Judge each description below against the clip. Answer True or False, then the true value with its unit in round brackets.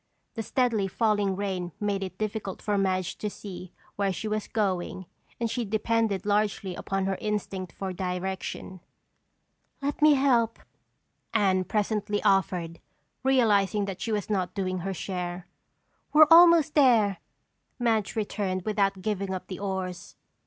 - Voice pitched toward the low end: False (200 Hz)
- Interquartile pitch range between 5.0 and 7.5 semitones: False (2.6 semitones)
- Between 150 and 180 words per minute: False (140 wpm)